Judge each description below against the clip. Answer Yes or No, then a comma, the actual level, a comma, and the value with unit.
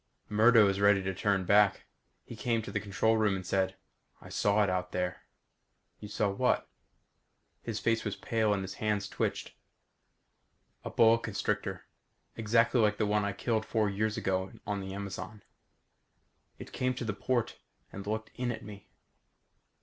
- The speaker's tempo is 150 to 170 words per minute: Yes, average, 165 wpm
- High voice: No, low, 105 Hz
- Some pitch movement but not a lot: No, narrow, 2.2 semitones